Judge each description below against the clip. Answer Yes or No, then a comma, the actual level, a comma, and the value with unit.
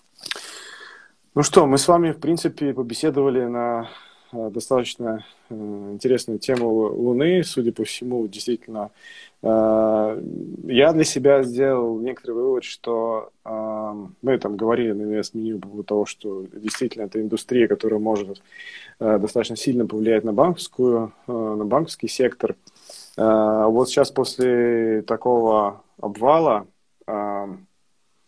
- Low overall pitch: Yes, low, 115 Hz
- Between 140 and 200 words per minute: No, average, 125 wpm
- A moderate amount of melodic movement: Yes, average, 3.1 semitones